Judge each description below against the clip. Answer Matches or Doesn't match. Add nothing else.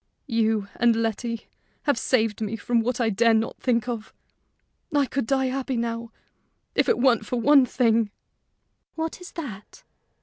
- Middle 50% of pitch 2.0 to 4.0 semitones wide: Matches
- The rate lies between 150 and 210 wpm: Matches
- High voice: Matches